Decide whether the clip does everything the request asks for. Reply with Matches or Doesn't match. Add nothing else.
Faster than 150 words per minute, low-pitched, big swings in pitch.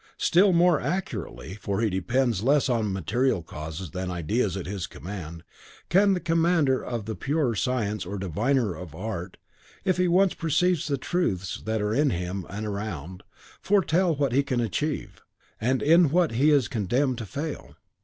Matches